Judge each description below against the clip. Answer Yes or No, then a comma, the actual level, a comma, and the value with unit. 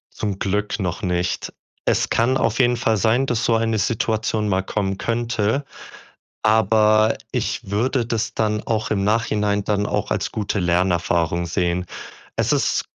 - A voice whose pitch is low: Yes, low, 105 Hz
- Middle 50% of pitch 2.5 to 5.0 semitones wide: Yes, average, 2.9 semitones